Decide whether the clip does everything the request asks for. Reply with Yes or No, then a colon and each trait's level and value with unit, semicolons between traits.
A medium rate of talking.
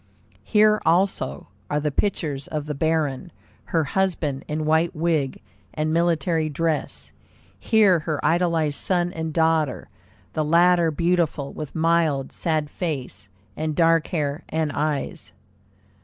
No: slow, 125 wpm